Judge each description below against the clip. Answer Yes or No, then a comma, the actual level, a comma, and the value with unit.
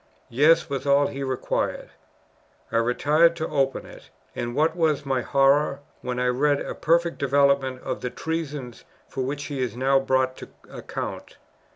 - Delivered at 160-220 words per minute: Yes, average, 165 wpm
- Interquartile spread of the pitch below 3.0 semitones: Yes, narrow, 2.4 semitones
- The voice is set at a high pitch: No, medium, 140 Hz